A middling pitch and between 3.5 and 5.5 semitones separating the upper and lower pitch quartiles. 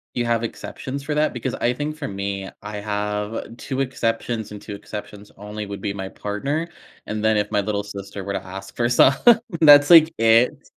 No: low, 110 Hz; average, 3.8 semitones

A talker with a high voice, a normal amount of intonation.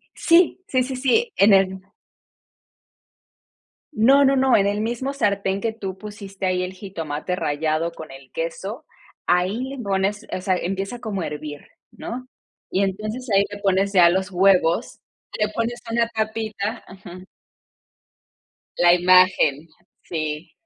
Yes: high, 195 Hz; average, 3.9 semitones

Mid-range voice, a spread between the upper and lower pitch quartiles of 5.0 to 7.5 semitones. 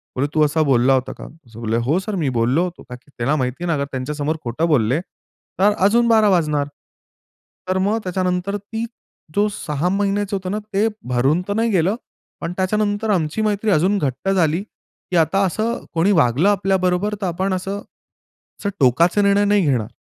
Yes: medium, 180 Hz; wide, 5.6 semitones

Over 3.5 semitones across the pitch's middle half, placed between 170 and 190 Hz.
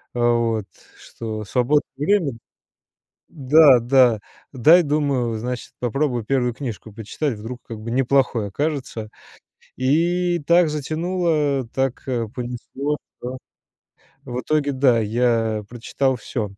No: average, 4.1 semitones; low, 130 Hz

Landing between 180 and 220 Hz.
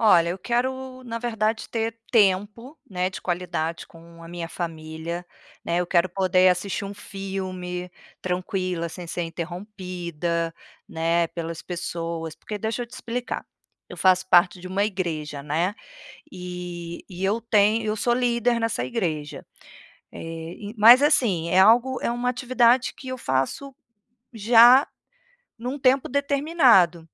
Yes: medium, 185 Hz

